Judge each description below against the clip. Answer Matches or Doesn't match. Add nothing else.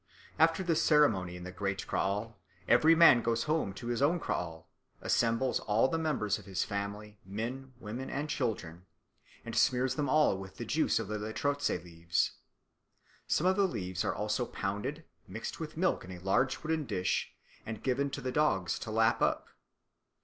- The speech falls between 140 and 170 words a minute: Doesn't match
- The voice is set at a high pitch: Doesn't match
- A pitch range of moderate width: Doesn't match